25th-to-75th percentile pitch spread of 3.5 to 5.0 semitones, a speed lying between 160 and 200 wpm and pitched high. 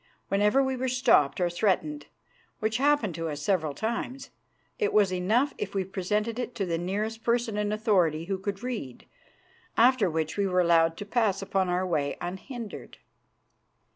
Yes: average, 4.7 semitones; average, 170 wpm; high, 200 Hz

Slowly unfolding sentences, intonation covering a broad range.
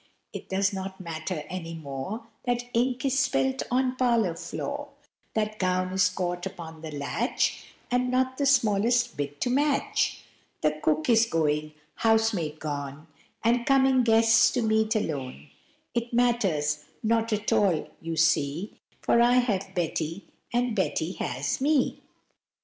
No: average, 145 wpm; wide, 6.9 semitones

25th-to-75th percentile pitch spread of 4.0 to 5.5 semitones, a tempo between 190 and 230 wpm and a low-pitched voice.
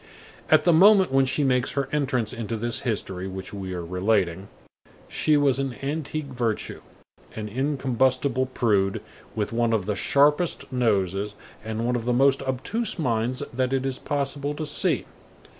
No: average, 4.3 semitones; average, 160 wpm; low, 125 Hz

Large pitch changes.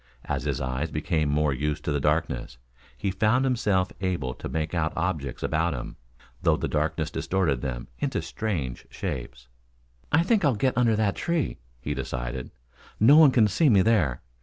Yes: wide, 7.9 semitones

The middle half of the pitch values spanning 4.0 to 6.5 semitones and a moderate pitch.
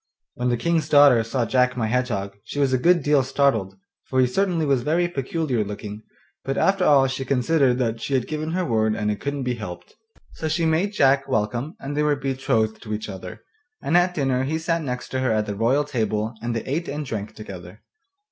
No: average, 4.9 semitones; low, 130 Hz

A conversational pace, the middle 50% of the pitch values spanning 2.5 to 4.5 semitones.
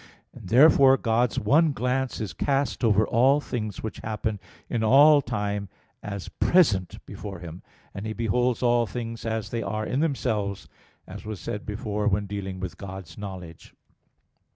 Yes: average, 160 wpm; average, 3.7 semitones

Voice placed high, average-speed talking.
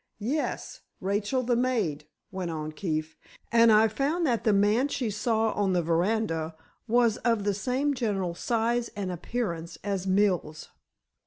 Yes: high, 210 Hz; average, 150 wpm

